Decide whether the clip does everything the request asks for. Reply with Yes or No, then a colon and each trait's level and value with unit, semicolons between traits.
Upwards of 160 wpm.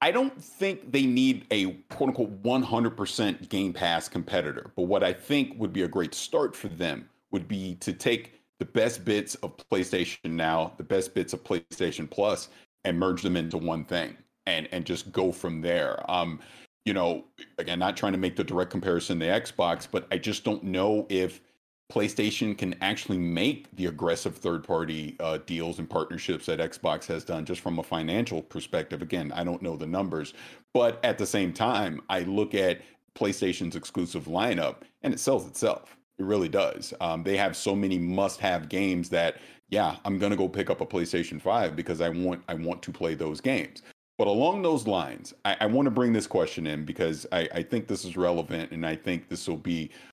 Yes: average, 200 wpm